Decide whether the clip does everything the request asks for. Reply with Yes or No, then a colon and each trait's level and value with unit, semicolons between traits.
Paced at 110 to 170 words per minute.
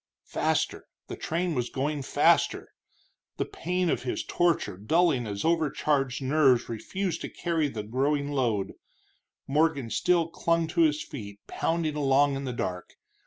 Yes: average, 145 wpm